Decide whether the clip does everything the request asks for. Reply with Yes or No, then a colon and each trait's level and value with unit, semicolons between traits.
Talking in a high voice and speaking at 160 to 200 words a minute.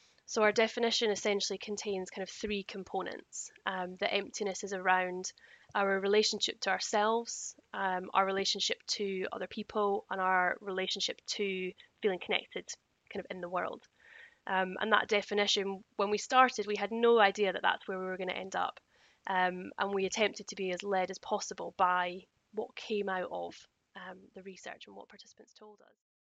Yes: high, 200 Hz; average, 180 wpm